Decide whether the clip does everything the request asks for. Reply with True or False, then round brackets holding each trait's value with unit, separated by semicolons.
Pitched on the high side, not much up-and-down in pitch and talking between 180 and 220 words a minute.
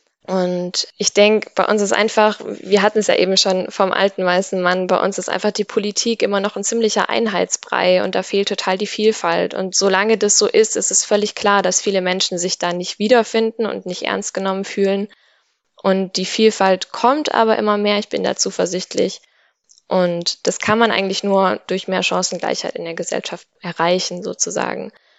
True (200 Hz; 2.3 semitones; 190 wpm)